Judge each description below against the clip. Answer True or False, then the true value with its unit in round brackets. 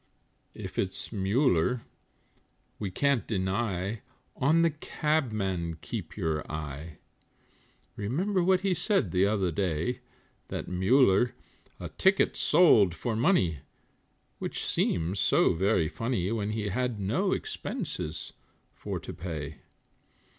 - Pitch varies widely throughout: True (7.2 semitones)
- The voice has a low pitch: True (105 Hz)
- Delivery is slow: True (115 wpm)